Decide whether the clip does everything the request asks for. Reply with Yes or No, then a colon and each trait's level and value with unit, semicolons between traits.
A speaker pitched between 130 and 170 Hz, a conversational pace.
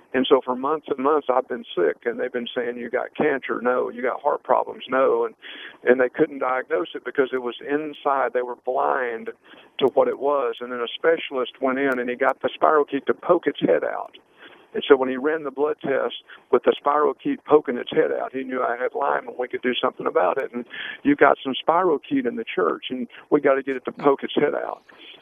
No: medium, 140 Hz; fast, 250 wpm